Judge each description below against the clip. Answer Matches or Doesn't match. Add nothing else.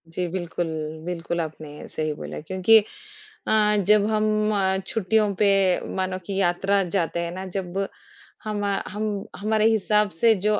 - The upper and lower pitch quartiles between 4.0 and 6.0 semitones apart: Doesn't match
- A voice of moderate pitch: Doesn't match